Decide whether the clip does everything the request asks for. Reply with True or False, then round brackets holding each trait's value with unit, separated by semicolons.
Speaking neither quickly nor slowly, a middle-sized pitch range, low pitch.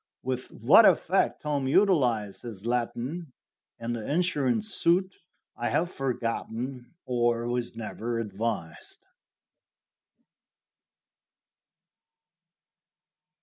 False (80 wpm; 4.0 semitones; 120 Hz)